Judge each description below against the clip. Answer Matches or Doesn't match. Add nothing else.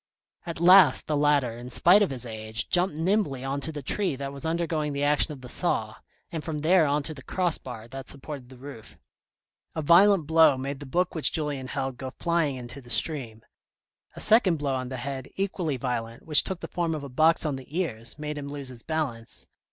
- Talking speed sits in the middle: Doesn't match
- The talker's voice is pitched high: Doesn't match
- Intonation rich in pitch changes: Doesn't match